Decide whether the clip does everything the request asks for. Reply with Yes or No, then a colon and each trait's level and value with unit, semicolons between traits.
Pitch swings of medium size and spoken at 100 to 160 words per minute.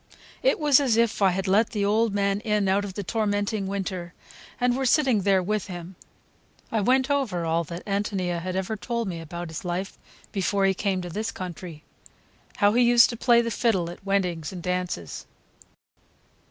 No: average, 3.7 semitones; average, 190 wpm